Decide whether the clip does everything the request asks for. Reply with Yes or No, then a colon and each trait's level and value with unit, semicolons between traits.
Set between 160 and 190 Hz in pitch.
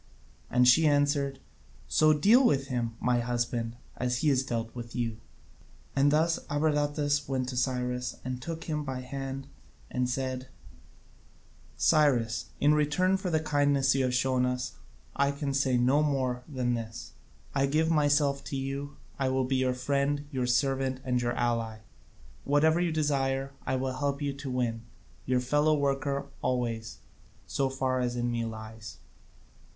No: low, 135 Hz